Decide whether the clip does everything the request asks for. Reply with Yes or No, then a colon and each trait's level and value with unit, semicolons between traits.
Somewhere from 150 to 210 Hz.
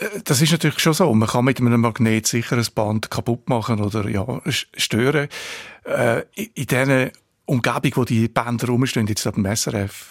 No: low, 120 Hz